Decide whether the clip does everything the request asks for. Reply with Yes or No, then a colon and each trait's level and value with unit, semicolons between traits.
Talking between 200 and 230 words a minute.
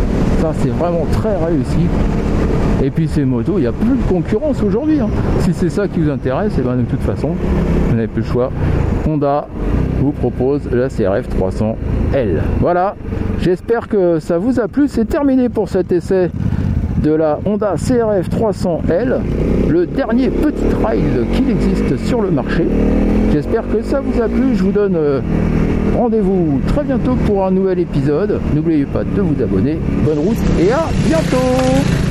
No: average, 170 wpm